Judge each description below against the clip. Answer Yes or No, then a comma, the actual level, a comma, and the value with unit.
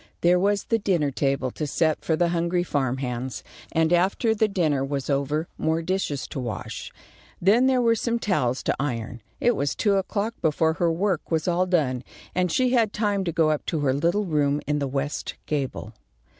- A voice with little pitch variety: No, wide, 5.5 semitones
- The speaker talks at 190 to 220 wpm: Yes, average, 200 wpm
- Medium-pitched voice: Yes, medium, 165 Hz